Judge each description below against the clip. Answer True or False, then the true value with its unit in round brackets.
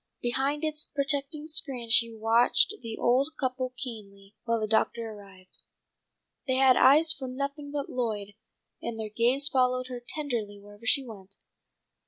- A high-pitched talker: True (250 Hz)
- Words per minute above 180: False (150 wpm)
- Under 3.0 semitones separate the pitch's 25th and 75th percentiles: False (3.9 semitones)